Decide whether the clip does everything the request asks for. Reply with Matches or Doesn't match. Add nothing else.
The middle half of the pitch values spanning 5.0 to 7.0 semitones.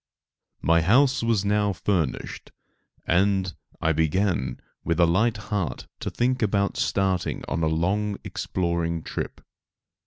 Doesn't match